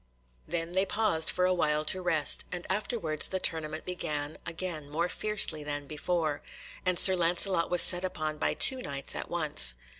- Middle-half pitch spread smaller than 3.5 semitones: Yes, average, 3.1 semitones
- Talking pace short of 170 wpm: No, average, 175 wpm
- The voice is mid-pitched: Yes, medium, 170 Hz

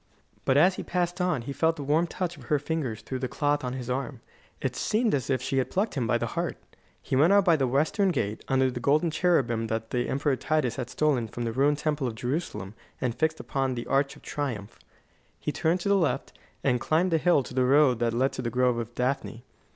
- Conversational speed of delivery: No, fast, 240 wpm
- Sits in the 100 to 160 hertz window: Yes, low, 135 Hz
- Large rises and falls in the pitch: No, average, 4.2 semitones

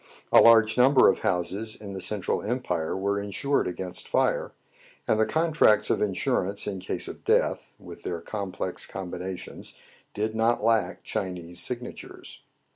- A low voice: Yes, low, 100 Hz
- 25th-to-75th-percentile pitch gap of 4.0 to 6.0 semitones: No, average, 3.5 semitones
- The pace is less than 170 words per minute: Yes, average, 145 wpm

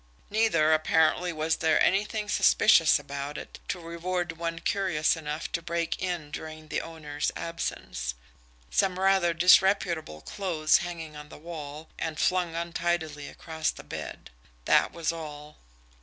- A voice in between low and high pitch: Yes, medium, 165 Hz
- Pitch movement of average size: No, narrow, 2.3 semitones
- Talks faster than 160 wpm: No, average, 140 wpm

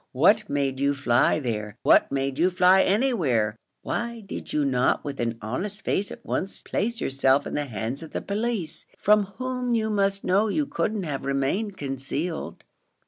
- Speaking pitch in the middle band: Yes, medium, 160 Hz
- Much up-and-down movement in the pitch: Yes, wide, 7.5 semitones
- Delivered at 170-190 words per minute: Yes, average, 175 wpm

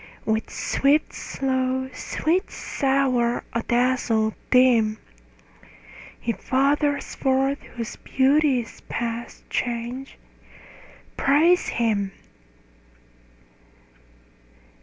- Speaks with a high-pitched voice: Yes, very high, 255 Hz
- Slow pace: Yes, slow, 70 wpm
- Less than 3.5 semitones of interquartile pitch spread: Yes, average, 2.8 semitones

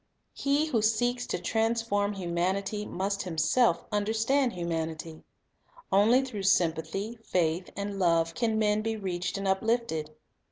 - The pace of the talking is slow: Yes, slow, 130 wpm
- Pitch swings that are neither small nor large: Yes, average, 4.3 semitones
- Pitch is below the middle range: No, high, 200 Hz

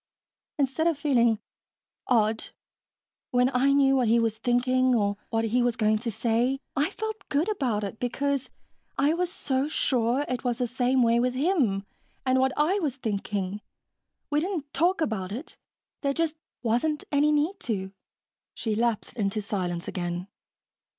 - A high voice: Yes, very high, 250 Hz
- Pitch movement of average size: Yes, average, 4.4 semitones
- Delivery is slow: No, average, 160 wpm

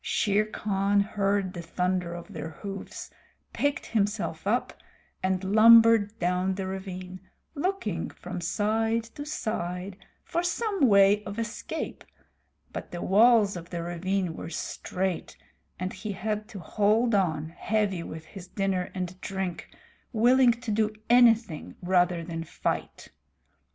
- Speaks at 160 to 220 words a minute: No, slow, 135 wpm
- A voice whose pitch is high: Yes, high, 195 Hz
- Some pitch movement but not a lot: Yes, average, 3.4 semitones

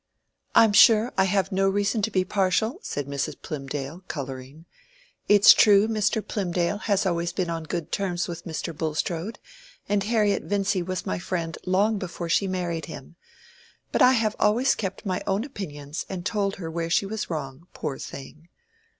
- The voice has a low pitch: No, medium, 185 Hz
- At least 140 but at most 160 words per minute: No, average, 175 wpm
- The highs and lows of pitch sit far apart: No, average, 3.7 semitones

